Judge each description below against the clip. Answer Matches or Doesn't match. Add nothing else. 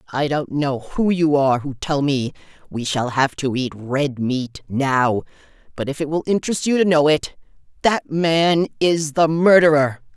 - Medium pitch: Matches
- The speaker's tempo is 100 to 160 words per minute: Doesn't match